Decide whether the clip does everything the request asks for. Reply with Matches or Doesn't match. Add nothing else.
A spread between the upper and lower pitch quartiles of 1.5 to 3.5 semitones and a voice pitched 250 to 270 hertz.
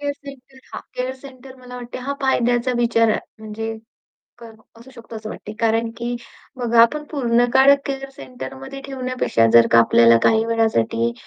Doesn't match